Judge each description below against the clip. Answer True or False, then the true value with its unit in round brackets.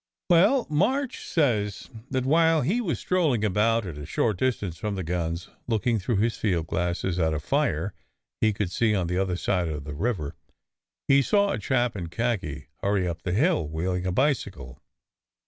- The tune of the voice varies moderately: False (6.9 semitones)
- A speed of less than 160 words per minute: False (180 wpm)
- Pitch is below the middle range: True (105 Hz)